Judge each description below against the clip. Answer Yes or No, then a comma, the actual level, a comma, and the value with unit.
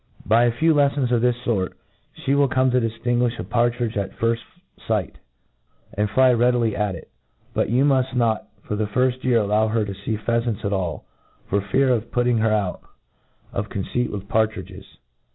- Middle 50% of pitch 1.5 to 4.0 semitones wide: Yes, average, 2.9 semitones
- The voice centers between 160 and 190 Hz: No, low, 115 Hz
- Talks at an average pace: Yes, average, 180 wpm